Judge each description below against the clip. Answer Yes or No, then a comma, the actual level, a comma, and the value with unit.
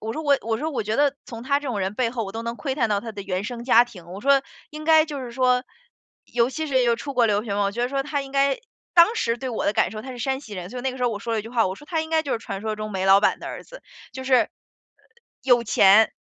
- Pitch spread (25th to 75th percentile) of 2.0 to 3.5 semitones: No, average, 4.3 semitones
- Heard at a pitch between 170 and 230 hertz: No, high, 240 Hz